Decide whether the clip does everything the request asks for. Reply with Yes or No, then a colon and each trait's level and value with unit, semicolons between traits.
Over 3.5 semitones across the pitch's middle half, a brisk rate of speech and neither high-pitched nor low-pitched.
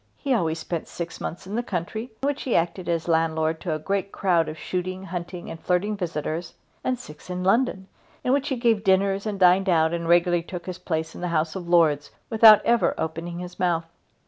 No: average, 3.1 semitones; fast, 215 wpm; medium, 180 Hz